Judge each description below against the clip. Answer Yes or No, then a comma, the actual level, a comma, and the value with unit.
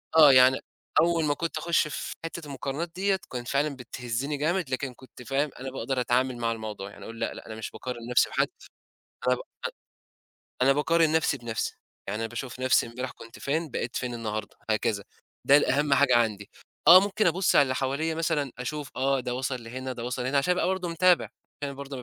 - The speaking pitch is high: No, low, 135 Hz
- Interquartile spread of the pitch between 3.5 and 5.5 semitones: Yes, average, 3.9 semitones